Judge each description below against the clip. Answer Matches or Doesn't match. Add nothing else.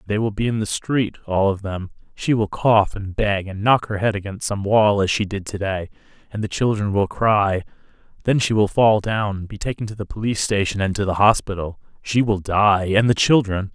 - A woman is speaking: Doesn't match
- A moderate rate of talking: Doesn't match